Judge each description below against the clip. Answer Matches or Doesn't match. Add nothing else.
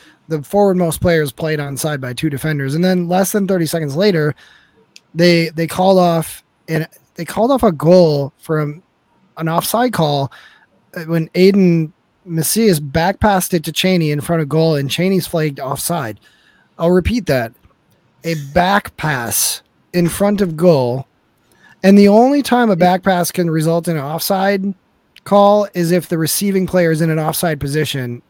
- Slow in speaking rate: Doesn't match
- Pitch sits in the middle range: Matches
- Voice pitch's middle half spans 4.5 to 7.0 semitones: Doesn't match